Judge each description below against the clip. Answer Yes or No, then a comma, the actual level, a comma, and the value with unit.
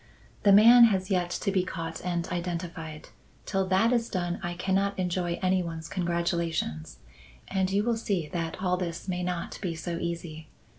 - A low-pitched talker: No, medium, 180 Hz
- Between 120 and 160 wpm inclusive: No, average, 175 wpm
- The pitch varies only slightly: Yes, narrow, 2.0 semitones